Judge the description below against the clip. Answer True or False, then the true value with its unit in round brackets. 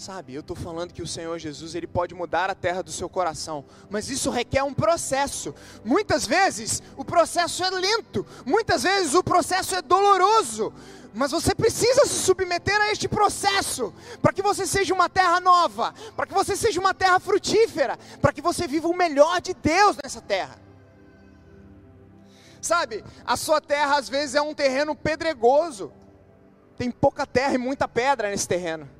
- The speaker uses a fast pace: False (170 wpm)